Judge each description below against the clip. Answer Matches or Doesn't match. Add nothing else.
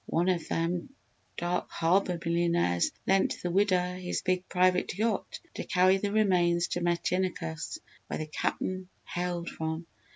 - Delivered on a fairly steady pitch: Matches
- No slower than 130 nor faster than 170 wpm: Matches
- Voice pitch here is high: Doesn't match